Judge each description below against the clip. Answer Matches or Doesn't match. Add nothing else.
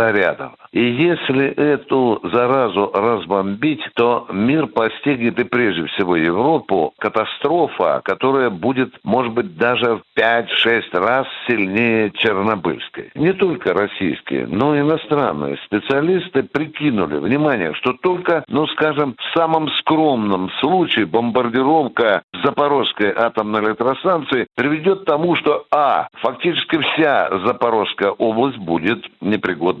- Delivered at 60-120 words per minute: Matches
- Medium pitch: Doesn't match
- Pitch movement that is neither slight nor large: Matches